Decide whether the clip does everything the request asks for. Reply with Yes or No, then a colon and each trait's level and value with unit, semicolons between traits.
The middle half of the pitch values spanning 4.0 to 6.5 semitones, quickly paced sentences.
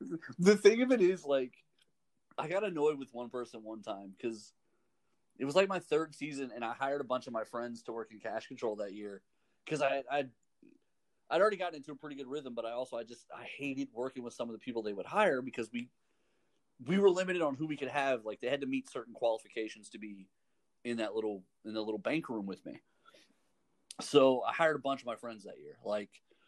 Yes: average, 4.8 semitones; fast, 235 wpm